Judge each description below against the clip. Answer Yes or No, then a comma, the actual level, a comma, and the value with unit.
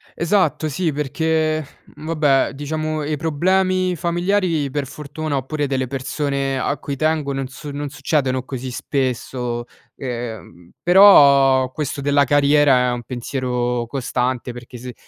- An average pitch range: Yes, average, 3.2 semitones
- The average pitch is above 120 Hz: Yes, medium, 140 Hz